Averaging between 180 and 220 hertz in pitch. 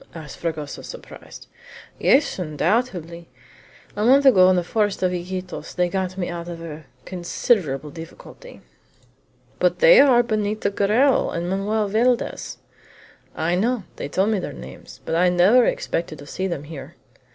Yes: medium, 185 Hz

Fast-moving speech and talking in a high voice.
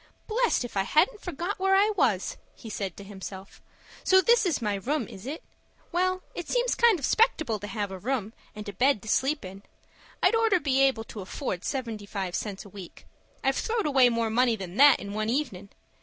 Yes: fast, 210 wpm; high, 245 Hz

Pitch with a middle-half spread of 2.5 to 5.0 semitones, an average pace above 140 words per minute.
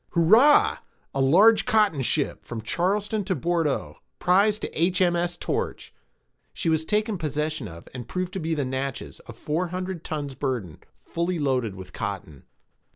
No: wide, 5.6 semitones; average, 155 wpm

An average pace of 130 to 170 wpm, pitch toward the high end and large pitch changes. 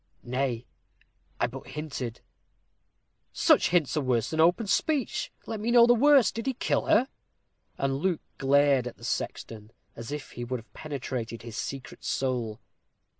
No: average, 160 wpm; medium, 140 Hz; wide, 7.3 semitones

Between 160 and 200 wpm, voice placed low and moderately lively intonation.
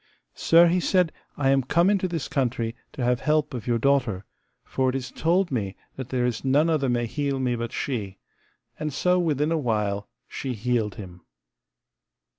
Yes: average, 185 wpm; low, 130 Hz; average, 4.6 semitones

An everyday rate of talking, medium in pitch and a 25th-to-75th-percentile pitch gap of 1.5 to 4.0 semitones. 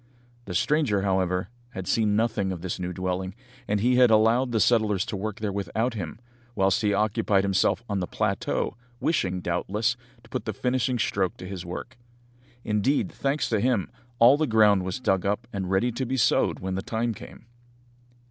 No: average, 185 wpm; low, 105 Hz; average, 3.6 semitones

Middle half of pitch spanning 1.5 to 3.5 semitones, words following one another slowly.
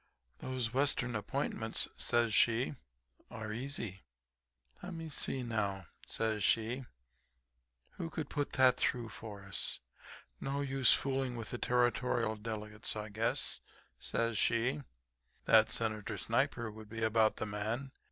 Yes: average, 3.1 semitones; slow, 125 wpm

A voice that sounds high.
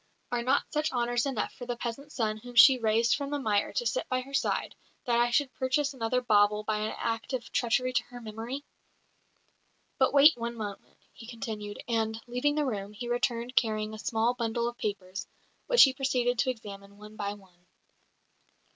Yes: high, 235 Hz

